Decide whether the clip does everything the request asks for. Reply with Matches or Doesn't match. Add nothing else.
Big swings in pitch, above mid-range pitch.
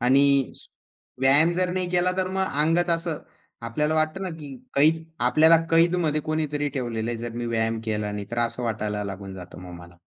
Doesn't match